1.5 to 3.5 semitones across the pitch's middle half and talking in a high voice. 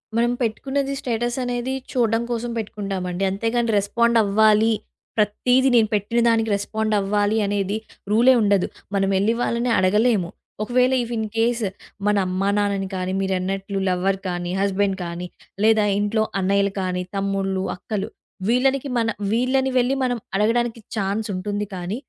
Yes: average, 3.2 semitones; high, 210 Hz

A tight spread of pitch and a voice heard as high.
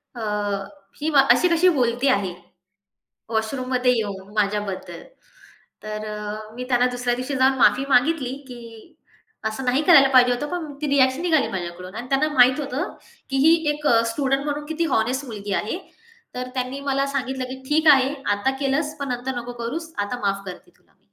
No: average, 3.7 semitones; very high, 255 Hz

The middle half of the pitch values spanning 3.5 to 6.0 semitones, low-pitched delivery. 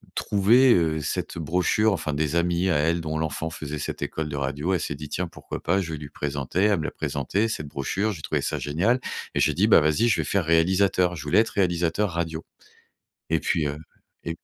Yes: average, 3.8 semitones; very low, 80 Hz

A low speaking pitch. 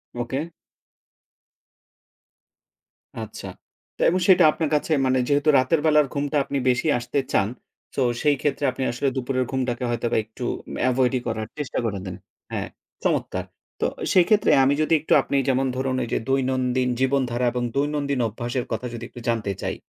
Yes: low, 130 Hz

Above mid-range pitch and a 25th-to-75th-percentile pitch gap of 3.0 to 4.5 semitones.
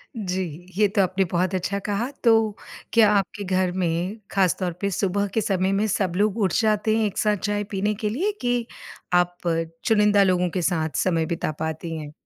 No: high, 195 Hz; narrow, 2.6 semitones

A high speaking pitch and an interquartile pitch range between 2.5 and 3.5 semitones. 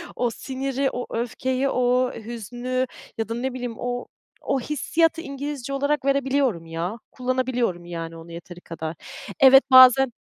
Yes: very high, 250 Hz; average, 3.0 semitones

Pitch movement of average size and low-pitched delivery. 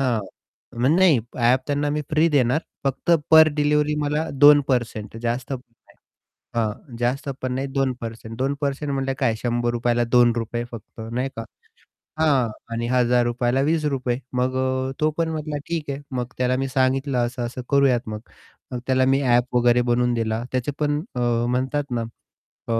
Yes: average, 3.0 semitones; low, 130 Hz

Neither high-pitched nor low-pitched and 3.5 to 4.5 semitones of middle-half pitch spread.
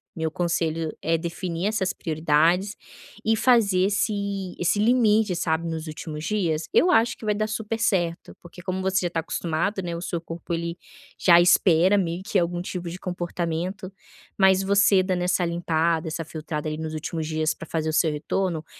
No: medium, 175 Hz; average, 3.0 semitones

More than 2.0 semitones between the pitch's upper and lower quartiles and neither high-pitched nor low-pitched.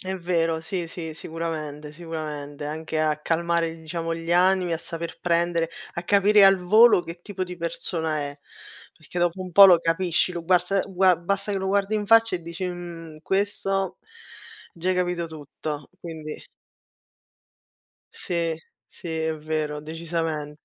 Yes: narrow, 2.4 semitones; medium, 170 Hz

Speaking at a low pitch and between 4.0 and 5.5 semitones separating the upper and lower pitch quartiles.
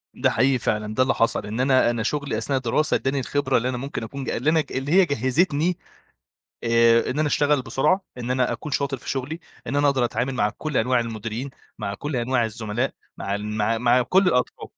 No: low, 130 Hz; average, 3.5 semitones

